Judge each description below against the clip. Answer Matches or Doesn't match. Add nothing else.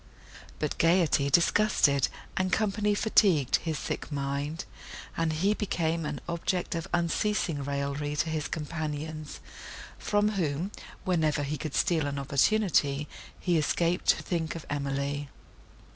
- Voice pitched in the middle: Matches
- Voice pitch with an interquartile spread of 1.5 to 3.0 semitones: Doesn't match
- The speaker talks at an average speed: Doesn't match